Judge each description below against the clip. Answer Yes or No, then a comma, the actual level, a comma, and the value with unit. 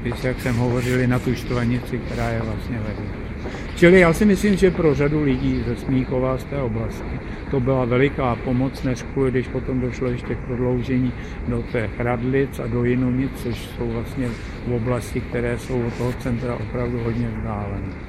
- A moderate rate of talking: No, fast, 180 wpm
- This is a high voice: No, low, 125 Hz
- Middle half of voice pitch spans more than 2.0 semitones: No, narrow, 1.5 semitones